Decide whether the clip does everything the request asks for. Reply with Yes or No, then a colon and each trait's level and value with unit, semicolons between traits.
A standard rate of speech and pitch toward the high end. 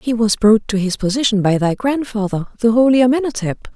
Yes: average, 190 wpm; high, 225 Hz